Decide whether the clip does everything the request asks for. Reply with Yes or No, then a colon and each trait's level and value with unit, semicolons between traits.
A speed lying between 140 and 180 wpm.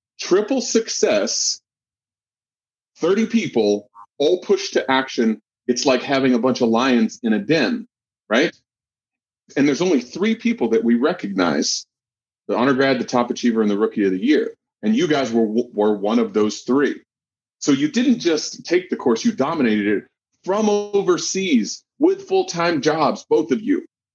Yes: average, 165 wpm